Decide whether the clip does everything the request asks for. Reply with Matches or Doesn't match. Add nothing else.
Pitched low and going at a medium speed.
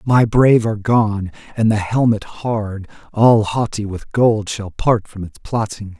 Matches